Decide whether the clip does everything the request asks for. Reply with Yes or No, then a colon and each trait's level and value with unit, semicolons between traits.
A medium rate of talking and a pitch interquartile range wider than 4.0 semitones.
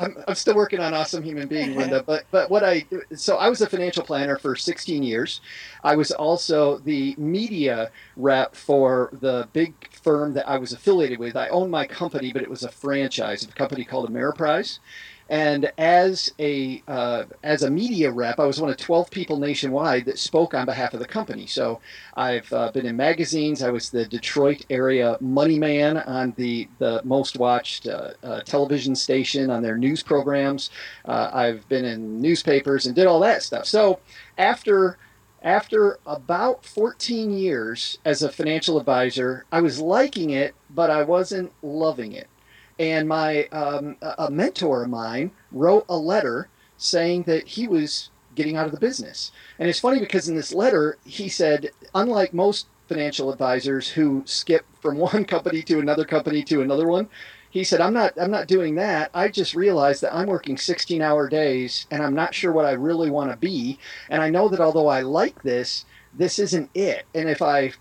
Yes: average, 185 wpm; average, 4.4 semitones